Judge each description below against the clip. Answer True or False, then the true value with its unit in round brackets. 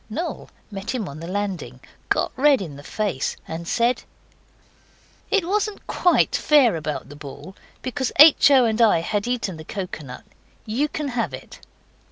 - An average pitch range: False (8.4 semitones)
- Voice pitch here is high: True (215 Hz)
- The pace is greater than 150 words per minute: True (165 wpm)